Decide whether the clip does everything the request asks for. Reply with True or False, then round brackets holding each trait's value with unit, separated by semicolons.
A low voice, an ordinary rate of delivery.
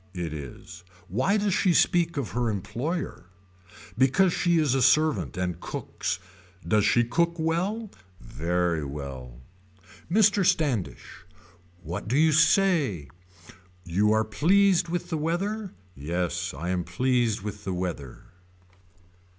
False (120 Hz; 125 wpm)